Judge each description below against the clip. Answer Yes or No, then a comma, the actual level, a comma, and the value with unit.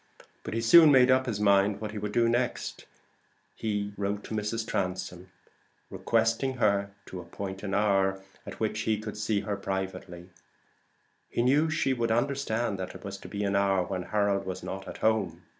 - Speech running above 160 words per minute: Yes, average, 185 wpm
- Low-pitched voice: Yes, low, 105 Hz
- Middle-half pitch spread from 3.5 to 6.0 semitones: No, average, 2.8 semitones